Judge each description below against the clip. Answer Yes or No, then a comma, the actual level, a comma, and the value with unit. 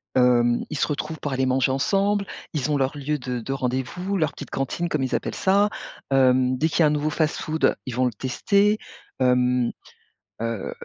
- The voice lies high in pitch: No, low, 135 Hz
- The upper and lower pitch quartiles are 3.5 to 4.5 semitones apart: Yes, average, 3.9 semitones